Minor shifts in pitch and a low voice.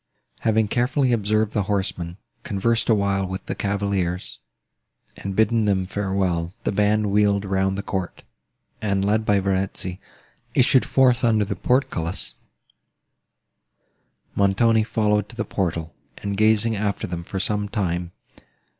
Yes: narrow, 2.3 semitones; low, 100 Hz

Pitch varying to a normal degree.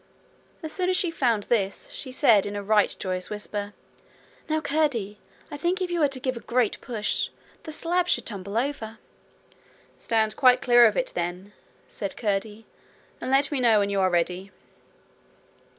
No: wide, 5.9 semitones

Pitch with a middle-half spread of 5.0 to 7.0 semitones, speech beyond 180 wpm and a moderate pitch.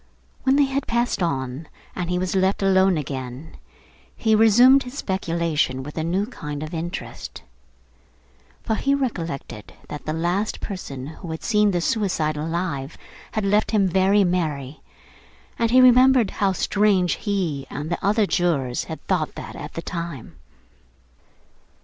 No: wide, 5.4 semitones; average, 150 wpm; medium, 180 Hz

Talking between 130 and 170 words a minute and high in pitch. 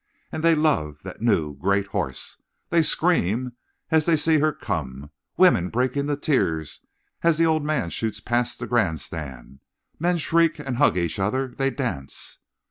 No: average, 165 wpm; low, 125 Hz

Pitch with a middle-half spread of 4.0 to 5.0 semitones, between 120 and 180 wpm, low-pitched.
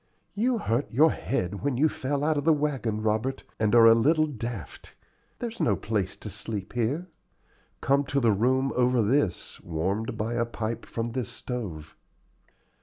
Yes: average, 4.5 semitones; average, 170 wpm; low, 120 Hz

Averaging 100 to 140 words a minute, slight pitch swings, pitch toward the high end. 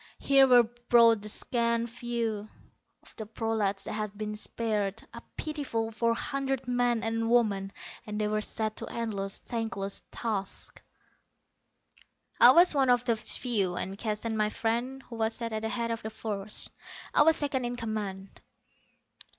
No: average, 160 wpm; narrow, 2.3 semitones; high, 225 Hz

